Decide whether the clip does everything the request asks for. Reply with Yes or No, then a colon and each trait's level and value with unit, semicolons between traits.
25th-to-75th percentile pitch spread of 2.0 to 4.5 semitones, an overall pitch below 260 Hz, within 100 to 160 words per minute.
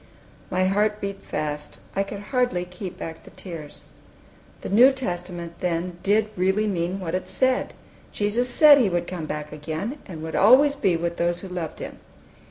No: average, 3.6 semitones; medium, 185 Hz; average, 180 wpm